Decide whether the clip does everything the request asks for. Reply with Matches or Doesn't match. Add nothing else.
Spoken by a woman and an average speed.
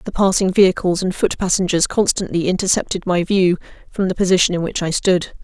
Matches